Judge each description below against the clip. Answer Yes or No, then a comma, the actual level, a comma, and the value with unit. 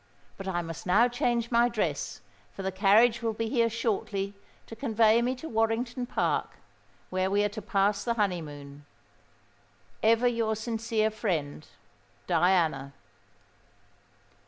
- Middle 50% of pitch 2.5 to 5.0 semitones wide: Yes, average, 3.6 semitones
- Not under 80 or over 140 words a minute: Yes, slow, 135 wpm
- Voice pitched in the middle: No, high, 215 Hz